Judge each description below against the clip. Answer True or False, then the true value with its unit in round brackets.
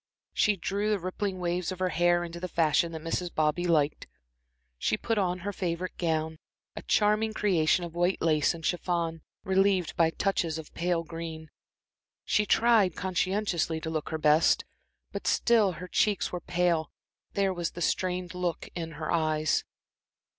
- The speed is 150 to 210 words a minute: True (165 wpm)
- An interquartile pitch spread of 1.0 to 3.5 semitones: True (2.4 semitones)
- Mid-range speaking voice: True (175 Hz)